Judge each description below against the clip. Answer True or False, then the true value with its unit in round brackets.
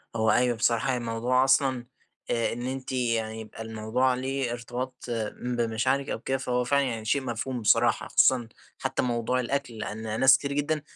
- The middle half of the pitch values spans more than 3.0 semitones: False (2.5 semitones)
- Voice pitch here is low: True (125 Hz)